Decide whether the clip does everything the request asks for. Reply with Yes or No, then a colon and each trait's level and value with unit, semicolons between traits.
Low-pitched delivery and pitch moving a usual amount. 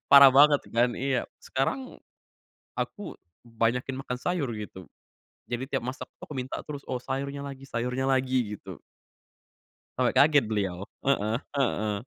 Yes: low, 130 Hz; average, 3.0 semitones